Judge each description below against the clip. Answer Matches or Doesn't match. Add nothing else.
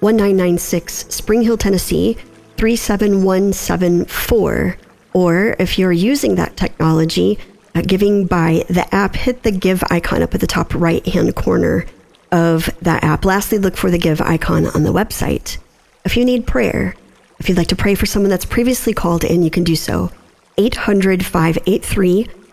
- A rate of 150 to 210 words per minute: Matches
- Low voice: Doesn't match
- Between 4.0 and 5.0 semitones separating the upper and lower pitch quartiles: Doesn't match